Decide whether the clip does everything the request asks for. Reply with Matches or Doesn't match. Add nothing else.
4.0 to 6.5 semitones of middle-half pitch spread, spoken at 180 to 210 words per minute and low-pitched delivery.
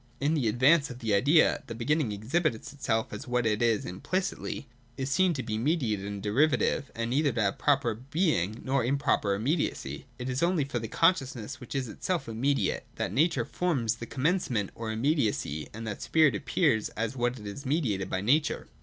Matches